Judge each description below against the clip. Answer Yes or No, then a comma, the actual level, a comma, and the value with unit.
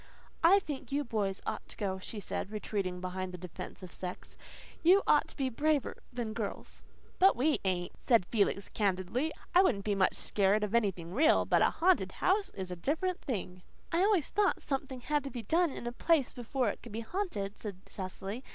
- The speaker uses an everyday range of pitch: No, wide, 7.6 semitones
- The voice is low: No, high, 230 Hz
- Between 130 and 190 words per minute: No, average, 200 wpm